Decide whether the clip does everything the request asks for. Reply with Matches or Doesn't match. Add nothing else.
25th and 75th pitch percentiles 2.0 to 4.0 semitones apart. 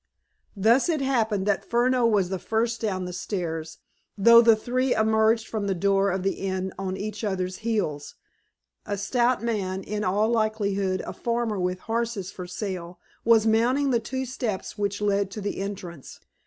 Matches